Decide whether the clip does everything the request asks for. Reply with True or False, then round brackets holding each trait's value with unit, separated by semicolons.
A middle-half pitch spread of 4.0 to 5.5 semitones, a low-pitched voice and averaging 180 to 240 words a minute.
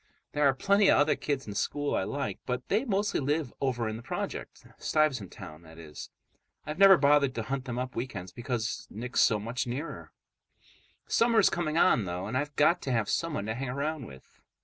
True (5.1 semitones; 130 Hz; 200 wpm)